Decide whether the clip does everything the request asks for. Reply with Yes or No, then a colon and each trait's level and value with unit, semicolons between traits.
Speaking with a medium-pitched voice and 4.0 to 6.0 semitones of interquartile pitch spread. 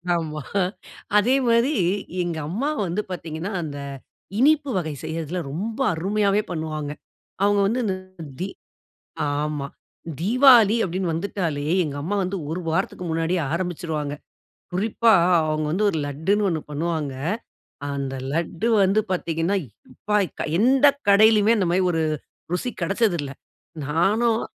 Yes: medium, 180 Hz; average, 4.9 semitones